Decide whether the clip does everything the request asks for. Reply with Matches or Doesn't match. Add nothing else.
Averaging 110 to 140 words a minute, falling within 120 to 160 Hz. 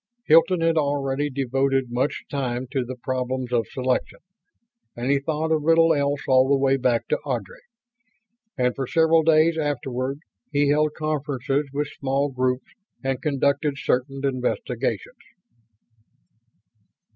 Matches